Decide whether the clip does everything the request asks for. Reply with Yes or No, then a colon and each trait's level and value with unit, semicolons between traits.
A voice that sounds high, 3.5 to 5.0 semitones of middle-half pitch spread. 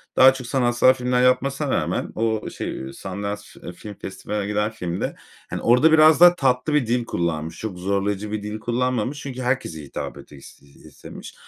No: low, 115 Hz; average, 4.4 semitones